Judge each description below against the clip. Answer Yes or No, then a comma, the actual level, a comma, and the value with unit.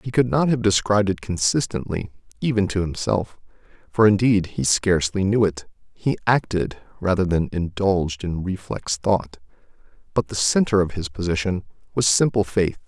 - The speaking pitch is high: No, very low, 95 Hz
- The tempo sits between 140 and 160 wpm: Yes, average, 155 wpm